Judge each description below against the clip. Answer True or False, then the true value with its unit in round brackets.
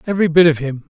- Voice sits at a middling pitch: True (165 Hz)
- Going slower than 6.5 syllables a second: False (8.0 syllables/s)